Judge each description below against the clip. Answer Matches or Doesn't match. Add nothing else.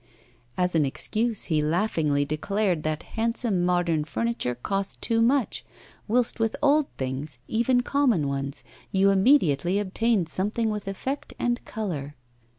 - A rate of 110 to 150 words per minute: Matches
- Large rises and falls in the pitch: Matches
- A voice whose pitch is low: Doesn't match